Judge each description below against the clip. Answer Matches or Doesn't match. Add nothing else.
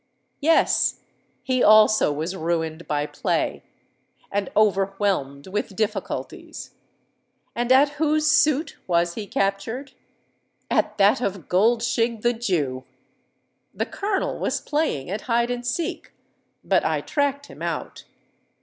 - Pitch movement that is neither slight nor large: Doesn't match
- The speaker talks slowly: Matches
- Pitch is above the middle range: Matches